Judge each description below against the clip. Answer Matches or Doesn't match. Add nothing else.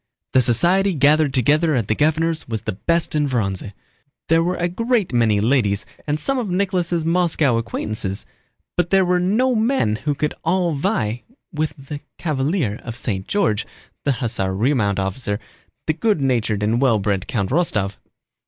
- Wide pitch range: Matches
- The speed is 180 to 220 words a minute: Doesn't match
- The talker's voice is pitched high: Doesn't match